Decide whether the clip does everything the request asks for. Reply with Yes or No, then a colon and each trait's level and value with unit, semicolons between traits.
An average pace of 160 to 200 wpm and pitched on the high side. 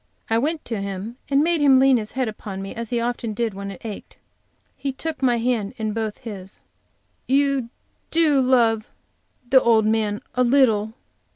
Yes: average, 180 wpm; high, 235 Hz